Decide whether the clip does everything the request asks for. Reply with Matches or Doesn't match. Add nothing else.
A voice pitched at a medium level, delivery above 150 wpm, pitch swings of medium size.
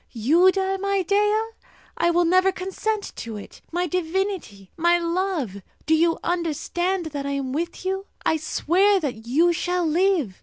Doesn't match